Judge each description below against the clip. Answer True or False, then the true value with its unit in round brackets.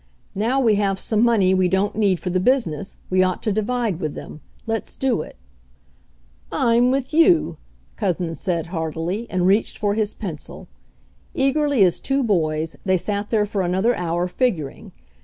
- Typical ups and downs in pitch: True (4.6 semitones)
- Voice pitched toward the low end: False (200 Hz)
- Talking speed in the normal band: True (165 wpm)